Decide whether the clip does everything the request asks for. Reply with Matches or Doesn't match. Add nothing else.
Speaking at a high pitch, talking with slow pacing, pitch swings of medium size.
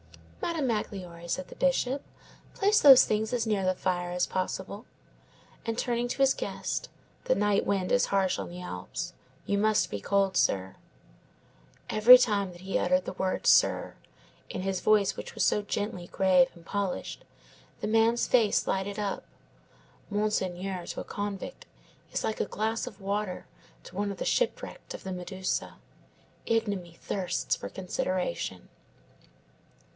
Doesn't match